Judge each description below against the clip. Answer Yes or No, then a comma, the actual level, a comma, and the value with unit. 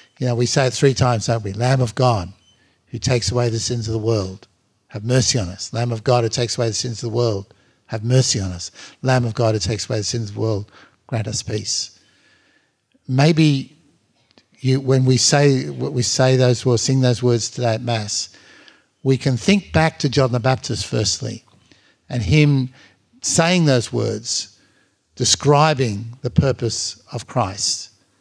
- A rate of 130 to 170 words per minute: No, average, 185 wpm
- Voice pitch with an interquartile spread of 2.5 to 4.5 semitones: Yes, average, 2.9 semitones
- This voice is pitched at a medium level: No, low, 120 Hz